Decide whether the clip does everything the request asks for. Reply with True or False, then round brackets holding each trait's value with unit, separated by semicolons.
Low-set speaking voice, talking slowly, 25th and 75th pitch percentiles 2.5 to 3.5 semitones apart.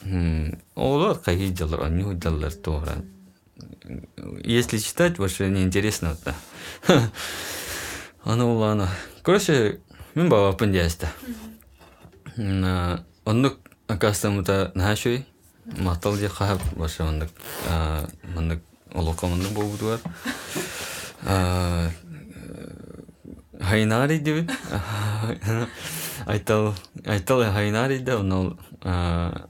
False (95 Hz; 90 wpm; 4.0 semitones)